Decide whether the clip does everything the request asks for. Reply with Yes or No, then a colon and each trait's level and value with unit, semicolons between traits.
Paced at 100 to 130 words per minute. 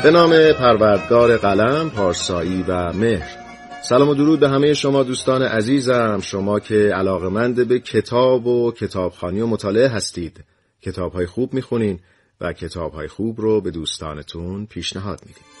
No: average, 140 wpm